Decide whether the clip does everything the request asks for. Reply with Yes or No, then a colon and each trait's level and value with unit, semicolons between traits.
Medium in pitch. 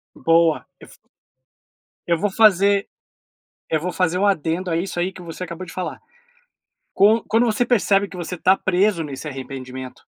Yes: medium, 180 Hz